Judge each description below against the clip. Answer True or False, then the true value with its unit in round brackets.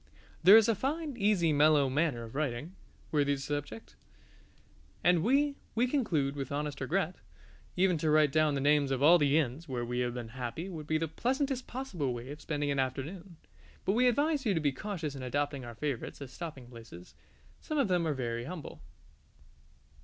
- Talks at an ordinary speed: True (190 wpm)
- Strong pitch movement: True (5.7 semitones)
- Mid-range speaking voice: True (150 Hz)